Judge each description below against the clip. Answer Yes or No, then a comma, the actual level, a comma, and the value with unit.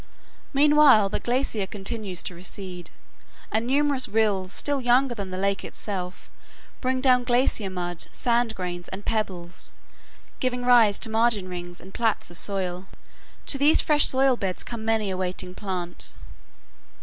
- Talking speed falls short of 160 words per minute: Yes, average, 150 wpm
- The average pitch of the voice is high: Yes, high, 215 Hz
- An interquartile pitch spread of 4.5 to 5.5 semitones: Yes, average, 5.0 semitones